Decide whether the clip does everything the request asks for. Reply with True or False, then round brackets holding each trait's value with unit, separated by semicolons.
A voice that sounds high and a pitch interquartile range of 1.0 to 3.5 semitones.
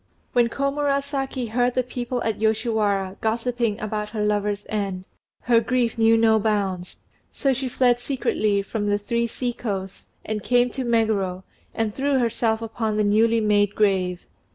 True (225 Hz; 2.9 semitones)